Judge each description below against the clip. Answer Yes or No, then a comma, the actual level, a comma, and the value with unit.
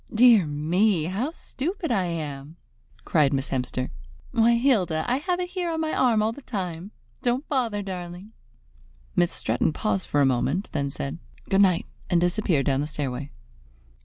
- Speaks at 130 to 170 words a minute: Yes, average, 165 wpm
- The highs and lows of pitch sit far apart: Yes, wide, 8.4 semitones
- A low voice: No, medium, 185 Hz